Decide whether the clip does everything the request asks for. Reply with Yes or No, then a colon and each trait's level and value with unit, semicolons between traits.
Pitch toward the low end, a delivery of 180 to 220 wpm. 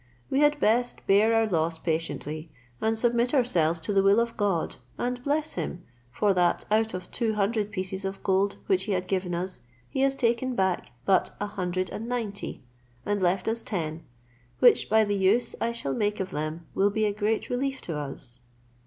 No: high, 200 Hz; average, 195 wpm